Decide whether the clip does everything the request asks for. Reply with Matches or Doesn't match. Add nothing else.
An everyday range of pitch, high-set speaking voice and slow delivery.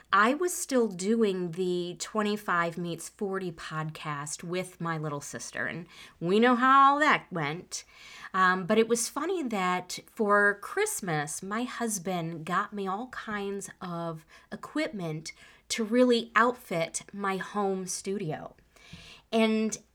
Matches